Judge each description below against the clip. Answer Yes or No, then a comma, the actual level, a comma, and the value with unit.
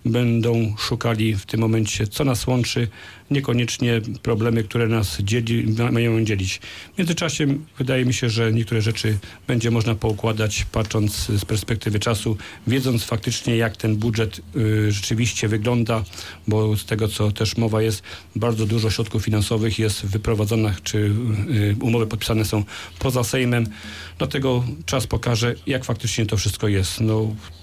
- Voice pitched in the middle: No, low, 110 Hz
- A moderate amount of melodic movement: No, narrow, 1.7 semitones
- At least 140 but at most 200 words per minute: Yes, average, 145 wpm